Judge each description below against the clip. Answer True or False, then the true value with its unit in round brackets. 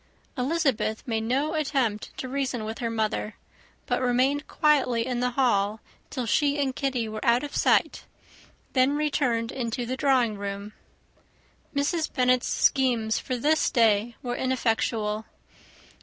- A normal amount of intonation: True (3.4 semitones)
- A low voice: False (250 Hz)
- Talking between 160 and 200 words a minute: False (140 wpm)